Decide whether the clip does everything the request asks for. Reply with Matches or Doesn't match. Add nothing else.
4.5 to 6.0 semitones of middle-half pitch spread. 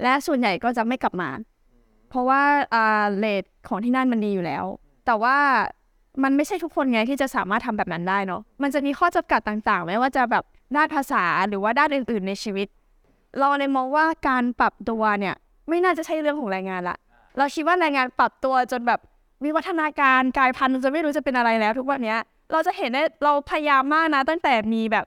Matches